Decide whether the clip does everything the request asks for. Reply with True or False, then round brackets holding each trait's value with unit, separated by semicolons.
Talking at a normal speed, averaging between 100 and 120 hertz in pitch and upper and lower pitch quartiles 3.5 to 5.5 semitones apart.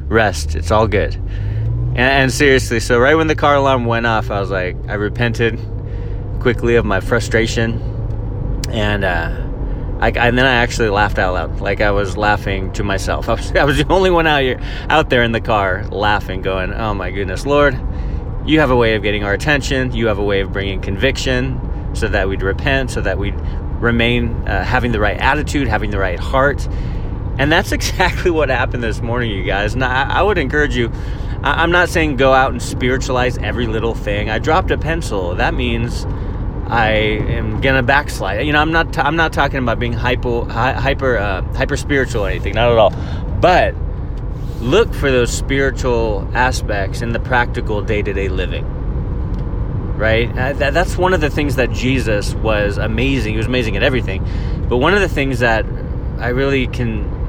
True (190 wpm; 115 Hz; 3.9 semitones)